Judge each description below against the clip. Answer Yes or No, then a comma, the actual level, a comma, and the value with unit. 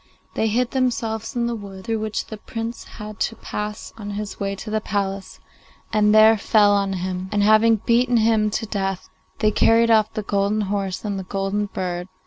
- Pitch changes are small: Yes, narrow, 2.0 semitones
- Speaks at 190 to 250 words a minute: Yes, average, 195 wpm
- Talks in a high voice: Yes, high, 210 Hz